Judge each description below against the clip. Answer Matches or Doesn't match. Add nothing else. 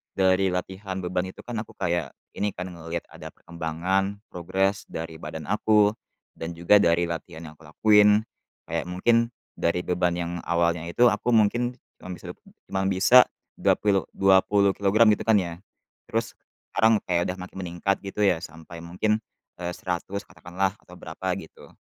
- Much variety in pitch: Doesn't match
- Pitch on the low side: Matches